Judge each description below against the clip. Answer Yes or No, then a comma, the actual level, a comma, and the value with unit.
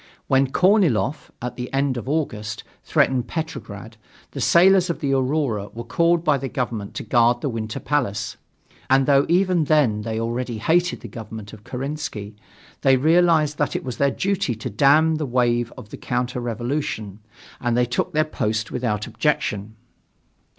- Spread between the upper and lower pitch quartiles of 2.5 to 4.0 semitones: No, average, 5.0 semitones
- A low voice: Yes, low, 125 Hz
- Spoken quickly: No, average, 165 wpm